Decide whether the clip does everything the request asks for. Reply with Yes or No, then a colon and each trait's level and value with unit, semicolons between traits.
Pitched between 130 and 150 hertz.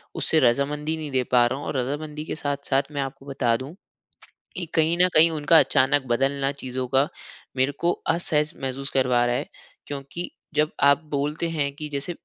Yes: medium, 140 Hz